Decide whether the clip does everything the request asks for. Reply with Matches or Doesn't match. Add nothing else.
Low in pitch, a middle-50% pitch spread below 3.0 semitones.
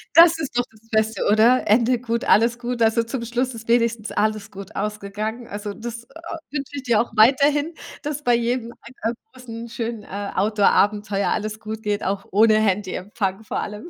Doesn't match